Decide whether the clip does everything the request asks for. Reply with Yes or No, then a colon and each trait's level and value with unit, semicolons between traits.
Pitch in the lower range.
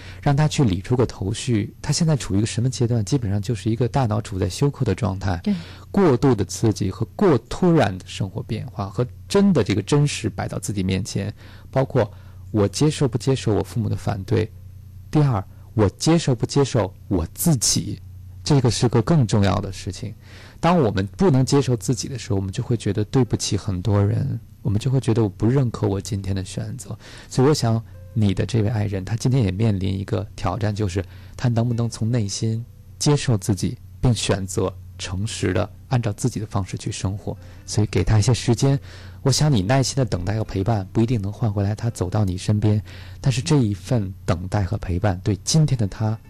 Yes: low, 105 Hz